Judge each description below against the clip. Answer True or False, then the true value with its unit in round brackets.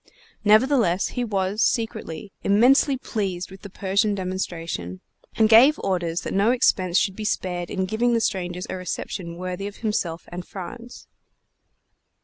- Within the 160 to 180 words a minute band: False (145 wpm)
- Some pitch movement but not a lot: True (3.5 semitones)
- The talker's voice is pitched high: True (195 Hz)